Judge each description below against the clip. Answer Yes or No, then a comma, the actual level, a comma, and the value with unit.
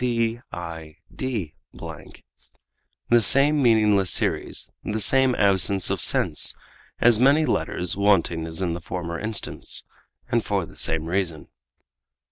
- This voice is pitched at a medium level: No, low, 100 Hz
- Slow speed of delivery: Yes, slow, 115 wpm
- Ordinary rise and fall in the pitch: No, wide, 5.8 semitones